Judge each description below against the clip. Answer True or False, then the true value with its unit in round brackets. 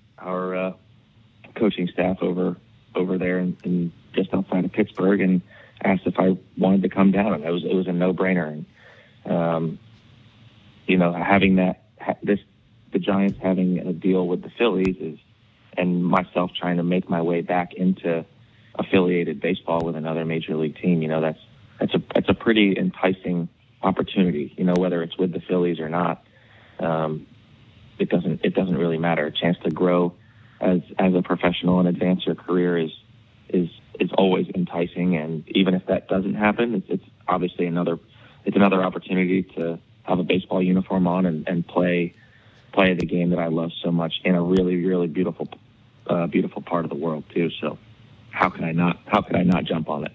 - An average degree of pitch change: False (1.9 semitones)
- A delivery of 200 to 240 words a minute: False (190 wpm)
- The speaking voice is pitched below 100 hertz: True (90 Hz)